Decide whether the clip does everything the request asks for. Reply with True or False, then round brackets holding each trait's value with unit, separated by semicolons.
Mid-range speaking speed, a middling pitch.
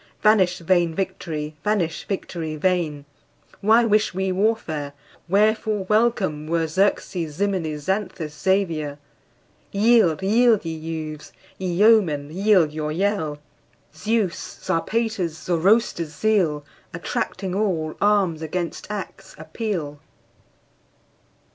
False (100 wpm; 180 Hz)